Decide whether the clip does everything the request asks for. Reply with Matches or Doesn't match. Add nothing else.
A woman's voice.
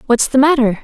Matches